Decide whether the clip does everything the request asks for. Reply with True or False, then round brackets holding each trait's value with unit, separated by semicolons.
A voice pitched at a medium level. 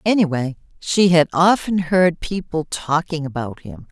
True (165 Hz)